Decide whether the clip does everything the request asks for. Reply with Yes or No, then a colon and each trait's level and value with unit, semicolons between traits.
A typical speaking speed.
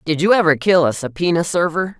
No: fast, 210 wpm